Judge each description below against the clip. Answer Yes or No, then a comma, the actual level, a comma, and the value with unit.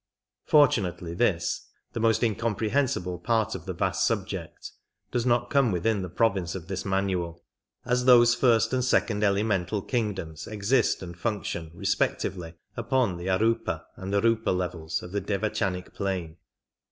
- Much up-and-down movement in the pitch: No, average, 4.3 semitones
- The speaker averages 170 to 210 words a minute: No, average, 140 wpm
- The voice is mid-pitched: No, low, 100 Hz